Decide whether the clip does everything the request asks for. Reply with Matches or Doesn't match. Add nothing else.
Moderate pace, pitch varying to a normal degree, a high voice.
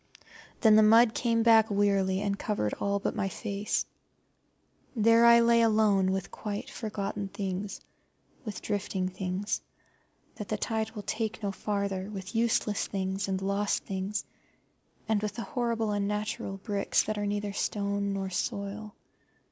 Doesn't match